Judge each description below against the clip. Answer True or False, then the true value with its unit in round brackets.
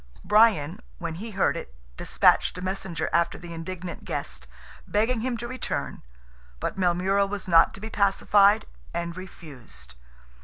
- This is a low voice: False (190 Hz)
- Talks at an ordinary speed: True (145 wpm)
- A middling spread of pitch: True (3.4 semitones)